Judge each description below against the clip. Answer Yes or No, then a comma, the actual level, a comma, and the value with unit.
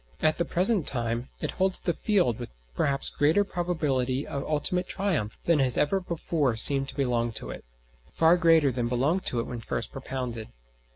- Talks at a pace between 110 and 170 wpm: No, average, 180 wpm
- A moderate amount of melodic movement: No, wide, 5.8 semitones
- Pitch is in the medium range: Yes, medium, 145 Hz